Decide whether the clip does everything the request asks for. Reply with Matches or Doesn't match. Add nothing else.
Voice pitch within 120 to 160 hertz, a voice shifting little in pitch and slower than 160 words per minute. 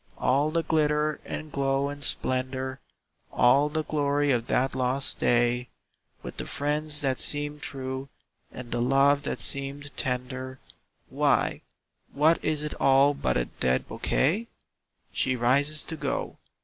Matches